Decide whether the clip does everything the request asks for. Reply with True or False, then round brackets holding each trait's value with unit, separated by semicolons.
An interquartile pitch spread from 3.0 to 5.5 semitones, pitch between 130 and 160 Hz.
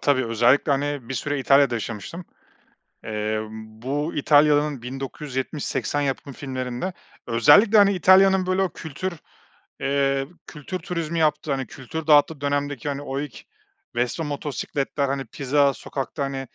False (2.4 semitones; 140 Hz)